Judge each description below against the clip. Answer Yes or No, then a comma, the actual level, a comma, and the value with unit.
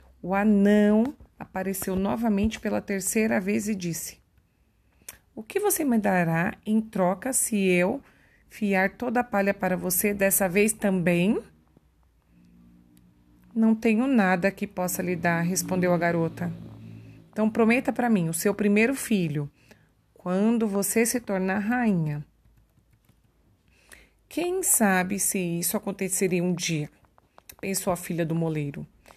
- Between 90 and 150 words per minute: Yes, average, 130 wpm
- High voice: Yes, high, 195 Hz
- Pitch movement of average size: Yes, average, 4.0 semitones